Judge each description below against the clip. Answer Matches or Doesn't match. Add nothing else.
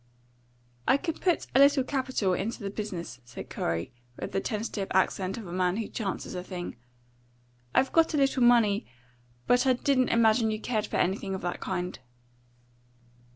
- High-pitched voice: Matches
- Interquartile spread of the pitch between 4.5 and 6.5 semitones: Matches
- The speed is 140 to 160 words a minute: Doesn't match